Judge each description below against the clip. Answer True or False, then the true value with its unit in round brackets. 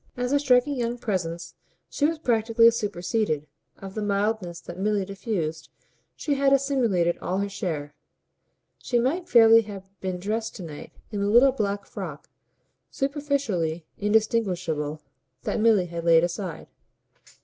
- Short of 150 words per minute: True (140 wpm)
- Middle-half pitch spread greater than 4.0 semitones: True (5.2 semitones)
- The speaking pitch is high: True (205 Hz)